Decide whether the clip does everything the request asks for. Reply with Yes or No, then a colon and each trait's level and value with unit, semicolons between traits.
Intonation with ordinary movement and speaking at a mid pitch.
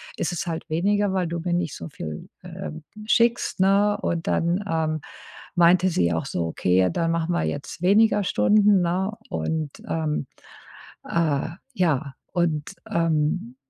Yes: average, 3.5 semitones; medium, 170 Hz